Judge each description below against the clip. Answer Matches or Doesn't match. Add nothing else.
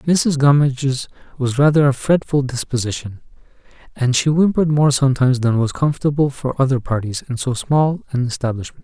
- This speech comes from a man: Matches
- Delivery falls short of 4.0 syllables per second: Doesn't match